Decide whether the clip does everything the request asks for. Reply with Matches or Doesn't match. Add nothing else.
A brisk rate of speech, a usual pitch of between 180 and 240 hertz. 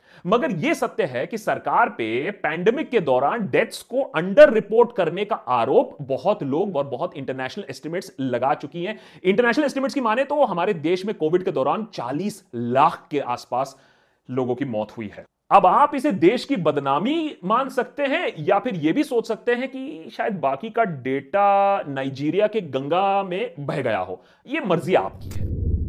Doesn't match